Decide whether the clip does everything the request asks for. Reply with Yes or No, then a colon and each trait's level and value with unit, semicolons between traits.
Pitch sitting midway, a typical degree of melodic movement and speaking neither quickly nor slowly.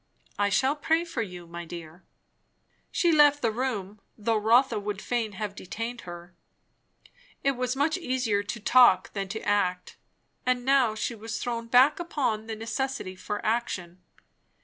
No: high, 225 Hz; average, 4.2 semitones; average, 155 wpm